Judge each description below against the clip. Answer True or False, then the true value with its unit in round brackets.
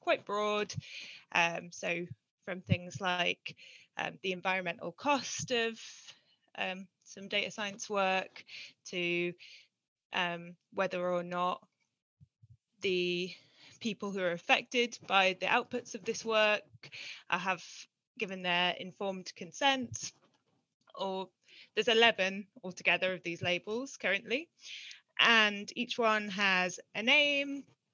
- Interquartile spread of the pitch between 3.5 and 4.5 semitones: True (3.9 semitones)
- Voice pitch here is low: False (190 Hz)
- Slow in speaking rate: True (115 wpm)